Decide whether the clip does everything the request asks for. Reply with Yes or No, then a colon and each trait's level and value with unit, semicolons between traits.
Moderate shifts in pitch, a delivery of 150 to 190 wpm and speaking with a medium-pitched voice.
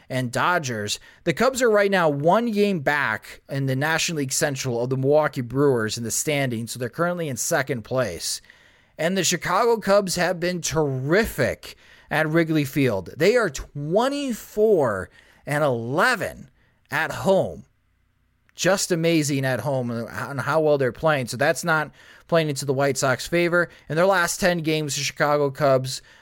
Yes: average, 4.9 semitones; average, 165 wpm; medium, 150 Hz